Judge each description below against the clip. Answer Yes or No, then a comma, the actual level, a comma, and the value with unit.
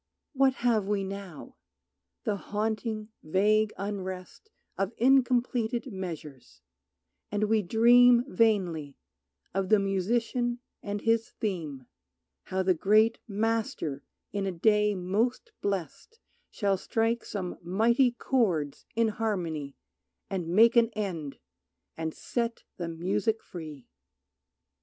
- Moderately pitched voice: No, high, 205 Hz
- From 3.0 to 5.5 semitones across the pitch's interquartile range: Yes, average, 3.9 semitones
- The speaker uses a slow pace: Yes, slow, 110 wpm